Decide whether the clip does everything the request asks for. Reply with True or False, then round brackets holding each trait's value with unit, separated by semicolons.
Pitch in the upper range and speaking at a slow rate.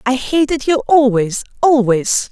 True (255 Hz; 130 wpm)